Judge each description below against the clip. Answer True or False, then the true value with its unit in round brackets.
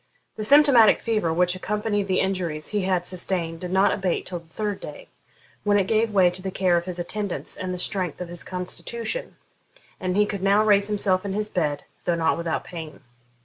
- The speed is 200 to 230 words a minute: True (205 wpm)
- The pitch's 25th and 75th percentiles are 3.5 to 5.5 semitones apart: False (2.9 semitones)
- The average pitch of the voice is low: False (185 Hz)